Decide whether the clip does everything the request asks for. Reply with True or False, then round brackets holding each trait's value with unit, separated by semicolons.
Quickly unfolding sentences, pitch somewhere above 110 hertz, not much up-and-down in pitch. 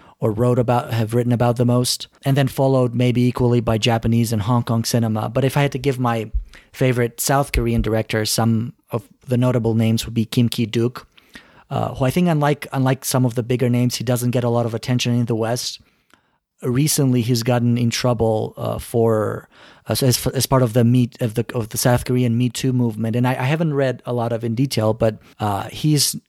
True (220 wpm; 120 Hz; 1.8 semitones)